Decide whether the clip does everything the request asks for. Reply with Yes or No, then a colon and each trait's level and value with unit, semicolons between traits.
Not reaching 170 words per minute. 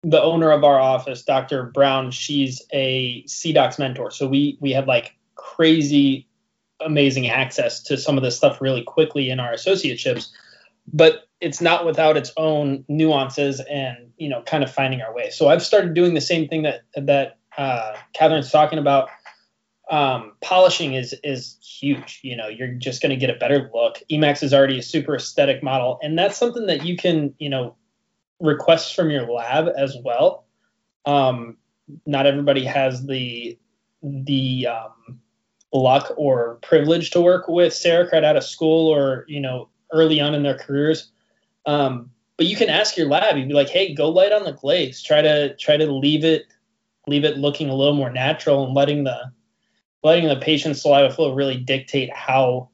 No: average, 180 wpm